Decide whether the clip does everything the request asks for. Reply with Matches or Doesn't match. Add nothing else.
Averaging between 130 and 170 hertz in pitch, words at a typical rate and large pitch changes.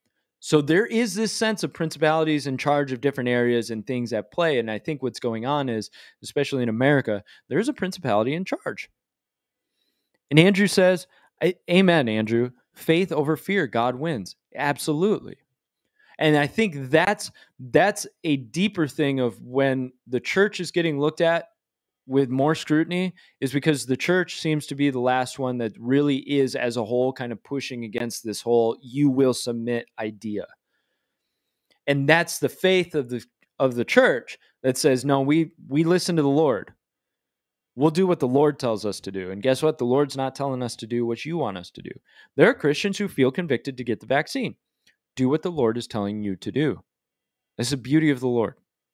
Doesn't match